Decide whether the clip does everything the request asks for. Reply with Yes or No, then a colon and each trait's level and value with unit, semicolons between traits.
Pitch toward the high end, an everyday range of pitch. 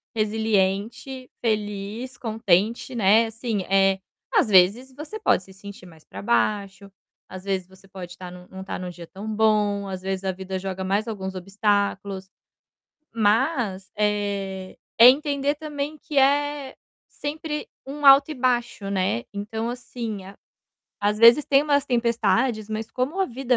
Yes: high, 210 Hz; average, 4.7 semitones